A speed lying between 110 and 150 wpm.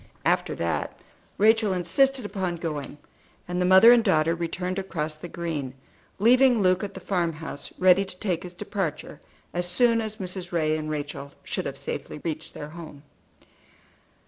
No: average, 165 wpm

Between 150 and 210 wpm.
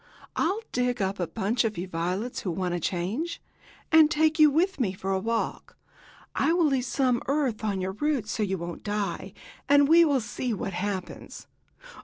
Yes: average, 190 wpm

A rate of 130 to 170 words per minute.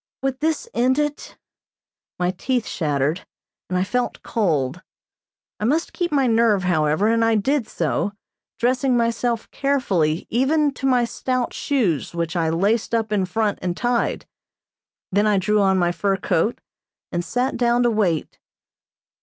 Yes: average, 155 wpm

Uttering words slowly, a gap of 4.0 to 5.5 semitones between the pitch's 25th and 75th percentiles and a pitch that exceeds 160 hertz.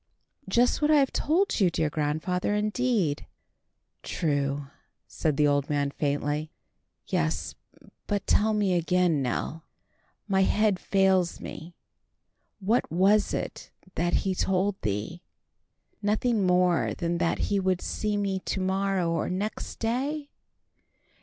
Yes: slow, 125 wpm; average, 4.5 semitones; medium, 185 Hz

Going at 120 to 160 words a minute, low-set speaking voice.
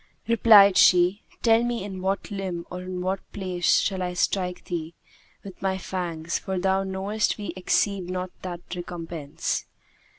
No: average, 155 wpm; medium, 185 Hz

